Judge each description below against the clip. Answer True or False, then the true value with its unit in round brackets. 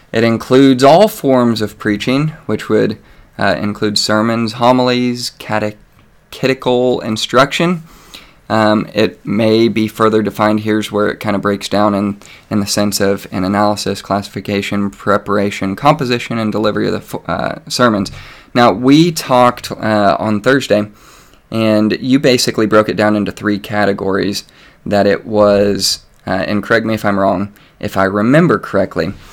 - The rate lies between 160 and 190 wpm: False (145 wpm)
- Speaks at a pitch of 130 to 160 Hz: False (105 Hz)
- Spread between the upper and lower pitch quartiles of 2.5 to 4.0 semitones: True (3.1 semitones)